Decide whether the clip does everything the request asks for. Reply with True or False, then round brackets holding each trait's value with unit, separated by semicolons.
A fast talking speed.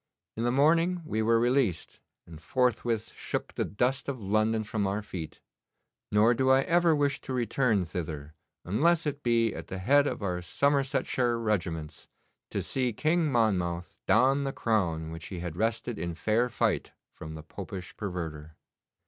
False (165 wpm)